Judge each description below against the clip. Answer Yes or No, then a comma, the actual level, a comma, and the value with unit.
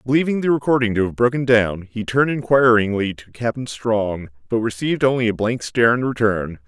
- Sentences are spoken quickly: No, average, 190 wpm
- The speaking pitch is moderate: No, low, 115 Hz